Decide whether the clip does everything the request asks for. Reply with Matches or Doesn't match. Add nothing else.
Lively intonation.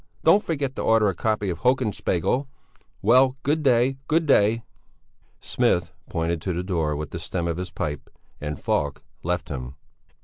Matches